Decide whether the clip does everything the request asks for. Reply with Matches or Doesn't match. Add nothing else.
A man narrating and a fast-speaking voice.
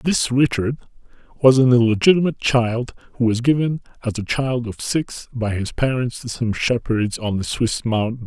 Doesn't match